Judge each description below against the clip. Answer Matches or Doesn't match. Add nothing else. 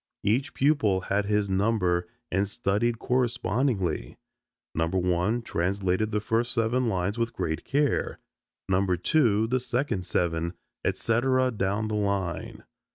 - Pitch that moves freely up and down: Doesn't match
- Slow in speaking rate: Matches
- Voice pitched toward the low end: Matches